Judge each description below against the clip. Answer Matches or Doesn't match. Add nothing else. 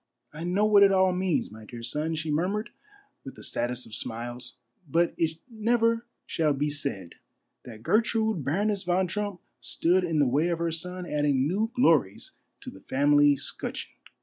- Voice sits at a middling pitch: Matches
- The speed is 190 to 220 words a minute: Doesn't match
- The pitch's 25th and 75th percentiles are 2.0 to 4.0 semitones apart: Doesn't match